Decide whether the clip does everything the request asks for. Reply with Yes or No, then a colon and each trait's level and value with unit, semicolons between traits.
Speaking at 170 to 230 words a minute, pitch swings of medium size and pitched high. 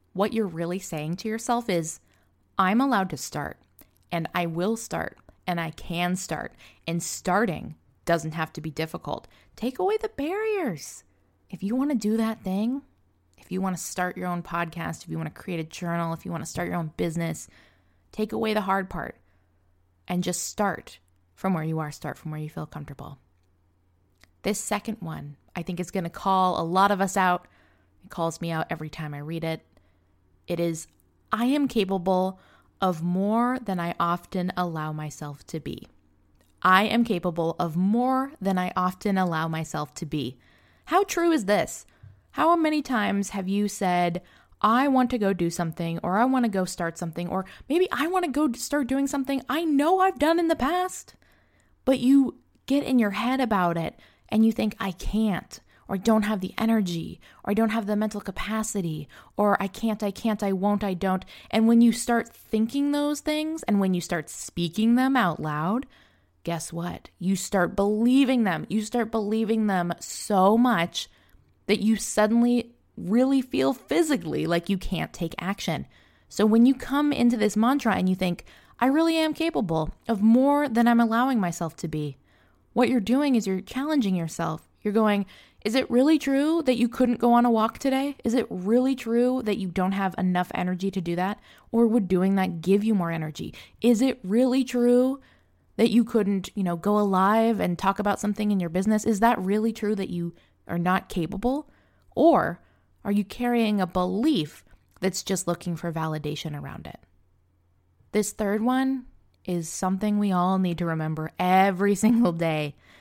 No: average, 190 wpm; wide, 5.7 semitones; high, 195 Hz